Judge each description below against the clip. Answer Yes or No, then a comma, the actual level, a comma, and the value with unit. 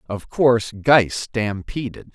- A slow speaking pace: Yes, slow, 110 wpm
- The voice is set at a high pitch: No, low, 115 Hz